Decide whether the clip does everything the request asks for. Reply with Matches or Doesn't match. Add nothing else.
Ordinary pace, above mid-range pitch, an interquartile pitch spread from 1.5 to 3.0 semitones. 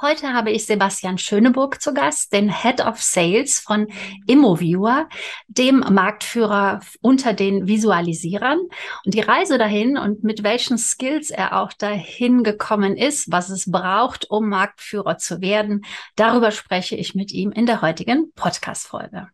Doesn't match